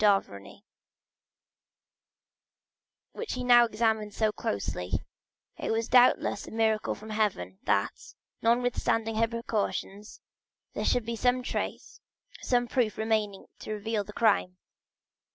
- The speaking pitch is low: No, high, 220 Hz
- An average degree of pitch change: No, narrow, 2.0 semitones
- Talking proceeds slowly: Yes, slow, 115 wpm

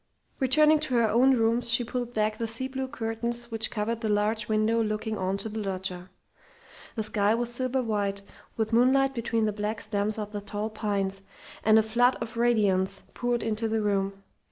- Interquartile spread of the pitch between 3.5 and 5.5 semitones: No, narrow, 2.4 semitones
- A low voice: No, high, 220 Hz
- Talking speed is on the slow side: No, average, 190 wpm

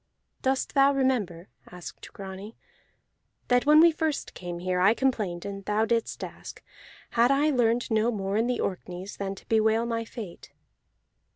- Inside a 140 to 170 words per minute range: Yes, average, 160 wpm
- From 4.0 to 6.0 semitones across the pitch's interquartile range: Yes, average, 4.4 semitones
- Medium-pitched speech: No, high, 220 Hz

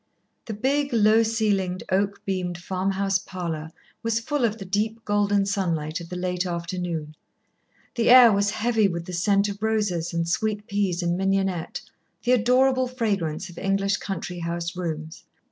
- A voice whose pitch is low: No, high, 195 Hz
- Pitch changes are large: No, average, 3.7 semitones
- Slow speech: No, average, 160 wpm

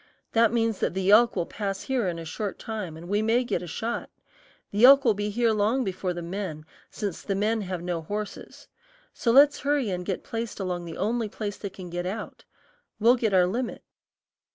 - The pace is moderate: No, fast, 210 wpm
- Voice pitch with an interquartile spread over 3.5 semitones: Yes, average, 3.9 semitones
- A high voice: Yes, high, 205 Hz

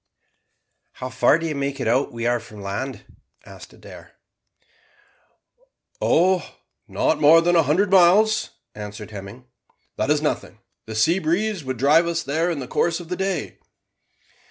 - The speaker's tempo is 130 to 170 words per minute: Yes, average, 165 wpm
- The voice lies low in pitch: No, medium, 150 Hz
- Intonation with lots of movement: Yes, wide, 6.1 semitones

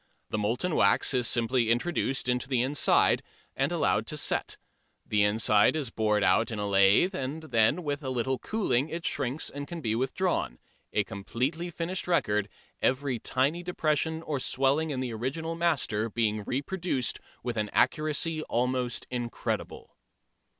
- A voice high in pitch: No, low, 130 Hz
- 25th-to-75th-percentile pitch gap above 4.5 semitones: Yes, wide, 5.6 semitones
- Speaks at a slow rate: No, average, 155 wpm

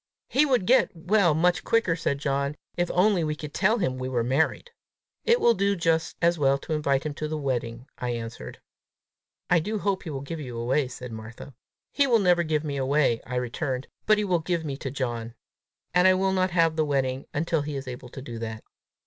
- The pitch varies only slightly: No, wide, 5.5 semitones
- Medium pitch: Yes, medium, 150 Hz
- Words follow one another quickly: Yes, fast, 220 wpm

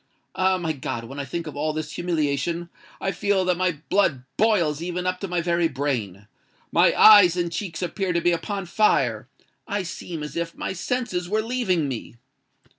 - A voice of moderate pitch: Yes, medium, 170 Hz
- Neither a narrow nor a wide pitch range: Yes, average, 3.8 semitones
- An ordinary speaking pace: Yes, average, 175 wpm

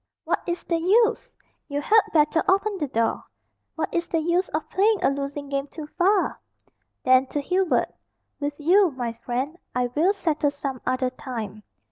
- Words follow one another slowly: No, average, 170 wpm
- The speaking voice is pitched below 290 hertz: No, very high, 295 Hz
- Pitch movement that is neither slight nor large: Yes, average, 5.0 semitones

